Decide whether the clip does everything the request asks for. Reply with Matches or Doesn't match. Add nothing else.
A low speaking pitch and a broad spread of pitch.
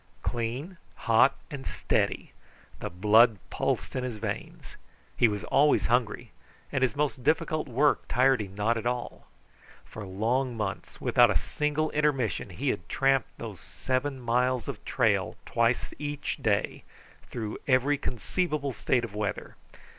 Doesn't match